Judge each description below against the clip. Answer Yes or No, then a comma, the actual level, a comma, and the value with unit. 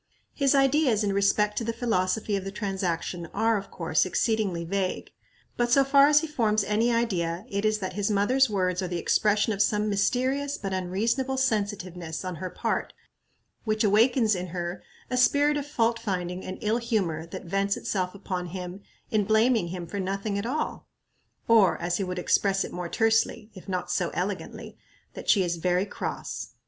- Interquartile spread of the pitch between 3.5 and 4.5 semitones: Yes, average, 3.9 semitones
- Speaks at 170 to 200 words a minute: Yes, average, 185 wpm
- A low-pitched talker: No, high, 200 Hz